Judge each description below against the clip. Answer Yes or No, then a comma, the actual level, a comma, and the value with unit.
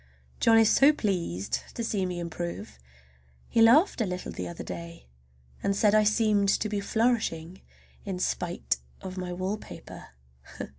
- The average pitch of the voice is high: Yes, high, 195 Hz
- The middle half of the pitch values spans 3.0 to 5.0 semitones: Yes, average, 4.2 semitones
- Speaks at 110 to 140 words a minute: No, average, 150 wpm